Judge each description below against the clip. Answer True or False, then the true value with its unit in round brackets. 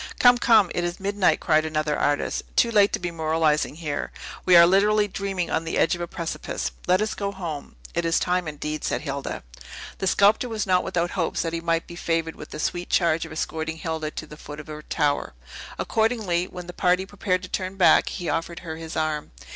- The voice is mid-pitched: True (170 Hz)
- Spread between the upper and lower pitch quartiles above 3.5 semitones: False (3.1 semitones)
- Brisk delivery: True (220 wpm)